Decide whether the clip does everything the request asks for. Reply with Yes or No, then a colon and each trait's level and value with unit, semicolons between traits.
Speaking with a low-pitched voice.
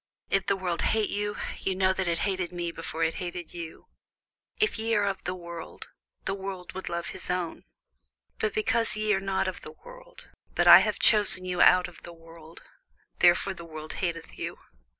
No: medium, 185 Hz